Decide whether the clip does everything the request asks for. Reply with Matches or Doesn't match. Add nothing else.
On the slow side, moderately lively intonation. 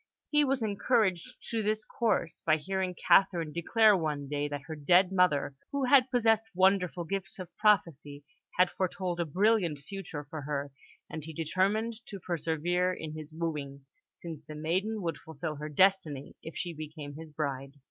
Doesn't match